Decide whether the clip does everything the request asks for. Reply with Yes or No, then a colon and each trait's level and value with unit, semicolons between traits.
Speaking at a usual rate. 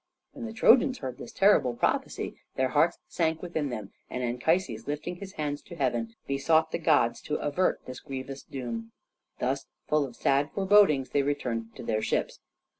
Yes: average, 175 wpm